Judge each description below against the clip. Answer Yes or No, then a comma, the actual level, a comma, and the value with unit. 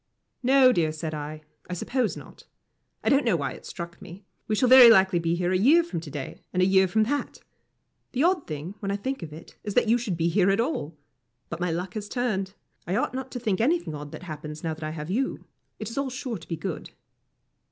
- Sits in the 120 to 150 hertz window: No, high, 190 Hz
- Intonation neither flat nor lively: No, wide, 6.8 semitones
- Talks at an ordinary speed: No, fast, 245 wpm